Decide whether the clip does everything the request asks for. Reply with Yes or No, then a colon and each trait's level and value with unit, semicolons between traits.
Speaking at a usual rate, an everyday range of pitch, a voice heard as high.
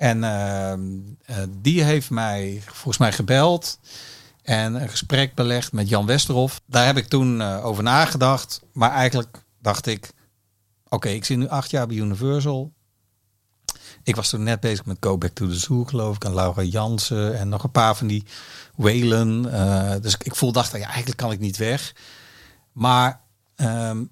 No: average, 180 wpm; average, 3.8 semitones; low, 115 Hz